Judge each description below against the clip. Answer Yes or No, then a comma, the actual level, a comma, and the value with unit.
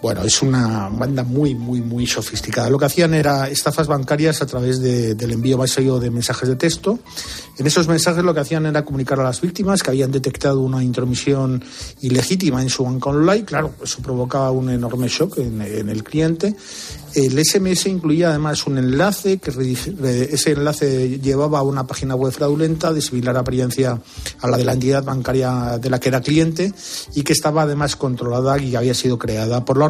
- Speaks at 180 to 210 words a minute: Yes, fast, 190 wpm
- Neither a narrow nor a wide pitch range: Yes, average, 3.2 semitones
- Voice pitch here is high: No, low, 135 Hz